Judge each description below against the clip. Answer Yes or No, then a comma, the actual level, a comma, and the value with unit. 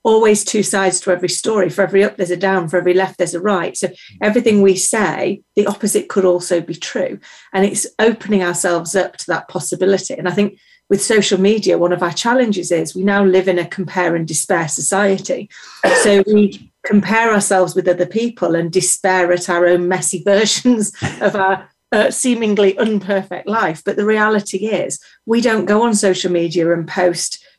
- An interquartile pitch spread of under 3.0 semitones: Yes, narrow, 2.6 semitones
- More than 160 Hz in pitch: Yes, high, 190 Hz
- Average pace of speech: Yes, average, 190 wpm